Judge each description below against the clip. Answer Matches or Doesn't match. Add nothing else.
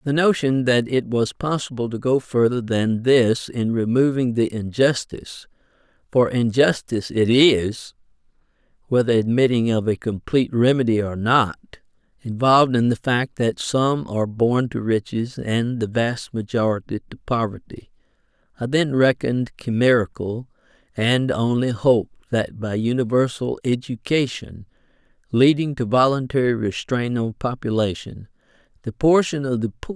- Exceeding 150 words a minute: Doesn't match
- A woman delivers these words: Doesn't match